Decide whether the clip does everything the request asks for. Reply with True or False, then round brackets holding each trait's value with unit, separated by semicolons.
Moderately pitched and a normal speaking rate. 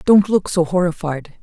True (175 Hz; 170 wpm)